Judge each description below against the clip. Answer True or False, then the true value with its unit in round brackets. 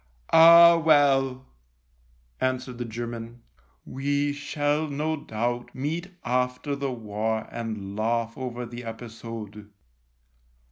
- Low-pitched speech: True (125 Hz)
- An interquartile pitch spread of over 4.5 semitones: False (4.0 semitones)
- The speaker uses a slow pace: True (110 wpm)